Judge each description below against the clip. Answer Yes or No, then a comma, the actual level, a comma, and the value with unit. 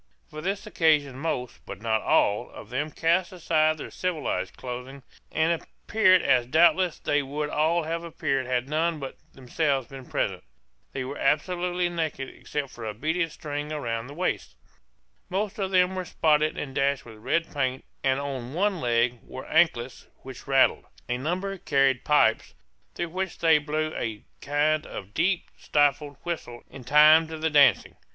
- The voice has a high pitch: No, medium, 150 Hz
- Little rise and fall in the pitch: No, average, 4.1 semitones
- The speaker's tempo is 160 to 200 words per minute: Yes, average, 165 wpm